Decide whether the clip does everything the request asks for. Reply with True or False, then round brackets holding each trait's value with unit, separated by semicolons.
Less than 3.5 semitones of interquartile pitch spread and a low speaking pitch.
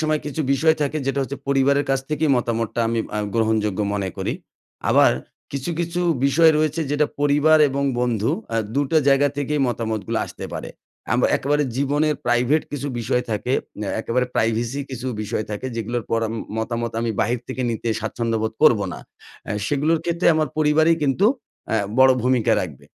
False (4.3 semitones; 130 Hz)